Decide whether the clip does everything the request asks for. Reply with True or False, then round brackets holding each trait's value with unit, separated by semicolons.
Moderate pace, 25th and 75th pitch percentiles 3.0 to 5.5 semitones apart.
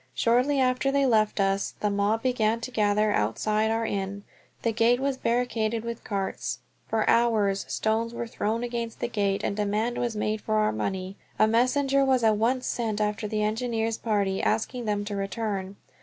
False (180 wpm; 2.4 semitones)